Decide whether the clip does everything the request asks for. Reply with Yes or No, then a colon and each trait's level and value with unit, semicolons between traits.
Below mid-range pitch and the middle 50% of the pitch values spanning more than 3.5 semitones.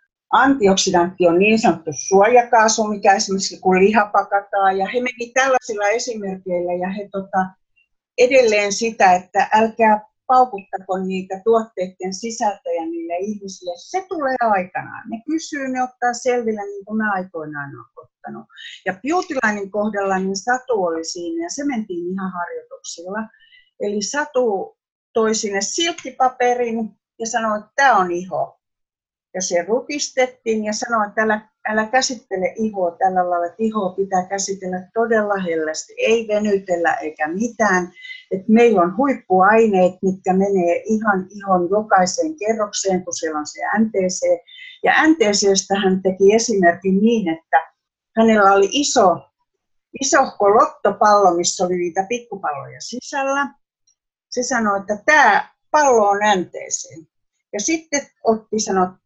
No: high, 210 Hz; average, 4.8 semitones